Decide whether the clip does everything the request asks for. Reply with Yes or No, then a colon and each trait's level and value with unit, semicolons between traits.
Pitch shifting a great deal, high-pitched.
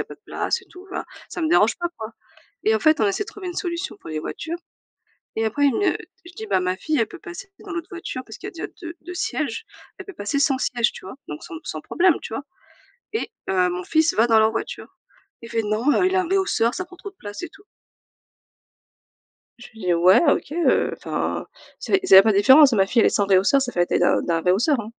Yes: wide, 8.9 semitones; very high, 260 Hz